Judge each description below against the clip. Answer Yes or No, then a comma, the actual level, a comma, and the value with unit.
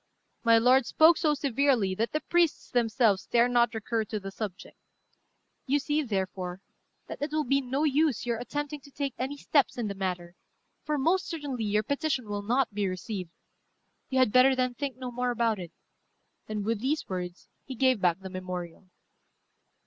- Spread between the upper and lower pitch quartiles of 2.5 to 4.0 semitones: No, wide, 5.4 semitones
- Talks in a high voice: Yes, high, 240 Hz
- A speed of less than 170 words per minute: No, average, 180 wpm